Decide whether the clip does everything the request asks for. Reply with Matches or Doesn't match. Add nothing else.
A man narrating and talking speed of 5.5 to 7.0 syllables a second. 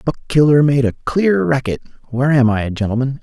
Matches